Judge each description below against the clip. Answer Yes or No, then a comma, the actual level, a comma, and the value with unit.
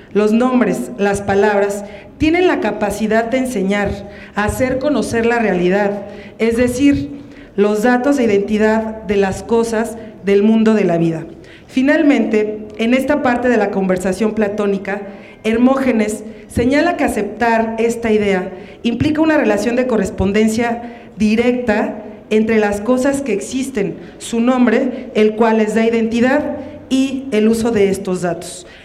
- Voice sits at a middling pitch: No, high, 220 Hz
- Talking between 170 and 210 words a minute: No, average, 135 wpm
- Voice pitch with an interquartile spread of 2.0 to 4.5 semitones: Yes, average, 3.4 semitones